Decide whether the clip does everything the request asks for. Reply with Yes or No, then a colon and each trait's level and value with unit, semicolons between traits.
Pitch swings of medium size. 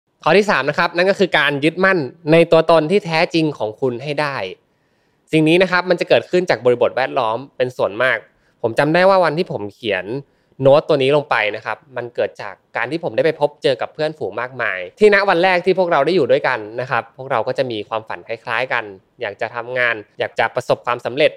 No: wide, 5.8 semitones